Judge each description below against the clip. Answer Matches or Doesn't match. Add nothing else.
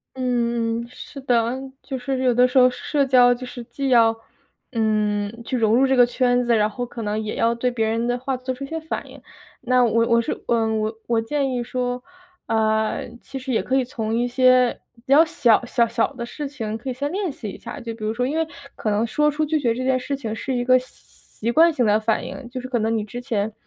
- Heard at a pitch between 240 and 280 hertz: Matches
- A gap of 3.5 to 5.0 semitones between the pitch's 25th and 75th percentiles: Doesn't match